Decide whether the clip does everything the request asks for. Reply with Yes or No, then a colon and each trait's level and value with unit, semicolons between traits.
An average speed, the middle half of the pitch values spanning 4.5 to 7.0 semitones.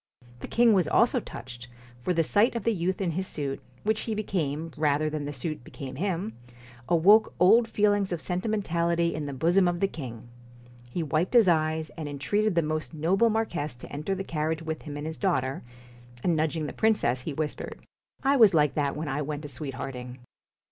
No: fast, 215 wpm; average, 4.9 semitones